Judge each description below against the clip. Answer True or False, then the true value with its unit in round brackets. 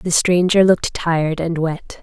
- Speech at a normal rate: True (175 wpm)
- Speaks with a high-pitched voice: False (170 Hz)